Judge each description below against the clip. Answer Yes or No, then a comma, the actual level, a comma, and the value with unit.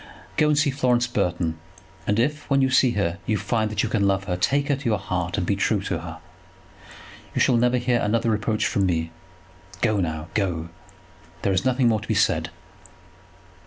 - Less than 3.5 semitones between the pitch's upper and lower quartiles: No, average, 5.1 semitones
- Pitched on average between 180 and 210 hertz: No, low, 105 Hz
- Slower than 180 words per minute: No, average, 200 wpm